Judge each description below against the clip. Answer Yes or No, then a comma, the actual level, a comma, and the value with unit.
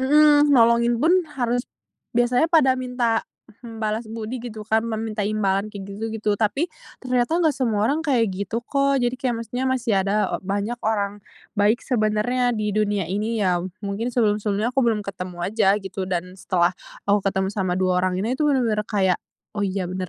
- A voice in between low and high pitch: No, high, 220 Hz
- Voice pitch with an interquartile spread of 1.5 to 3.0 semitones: No, average, 3.5 semitones